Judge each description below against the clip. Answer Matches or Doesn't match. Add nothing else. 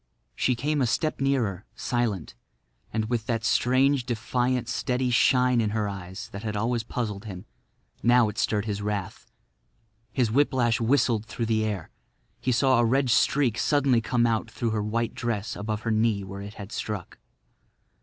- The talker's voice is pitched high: Doesn't match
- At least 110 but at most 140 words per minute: Doesn't match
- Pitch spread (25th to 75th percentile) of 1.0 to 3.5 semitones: Matches